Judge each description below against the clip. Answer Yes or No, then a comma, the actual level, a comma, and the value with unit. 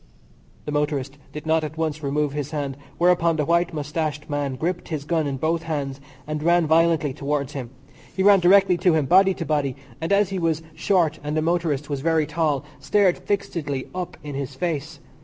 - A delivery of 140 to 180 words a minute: No, average, 195 wpm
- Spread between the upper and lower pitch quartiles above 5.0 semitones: No, average, 2.7 semitones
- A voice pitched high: No, medium, 155 Hz